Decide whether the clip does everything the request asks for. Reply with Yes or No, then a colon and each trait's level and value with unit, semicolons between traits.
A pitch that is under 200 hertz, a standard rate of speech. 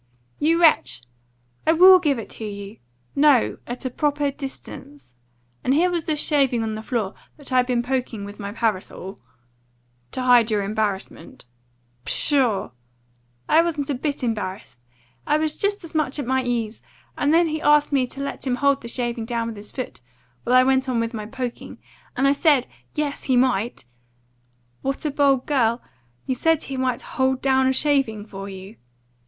No: very high, 255 Hz; average, 185 wpm